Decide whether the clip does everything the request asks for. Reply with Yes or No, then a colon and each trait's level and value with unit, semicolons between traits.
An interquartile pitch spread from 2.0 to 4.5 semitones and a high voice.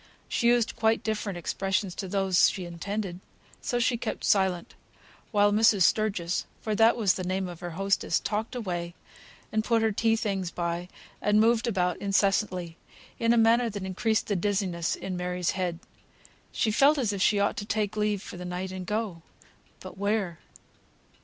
Yes: average, 3.4 semitones; high, 200 Hz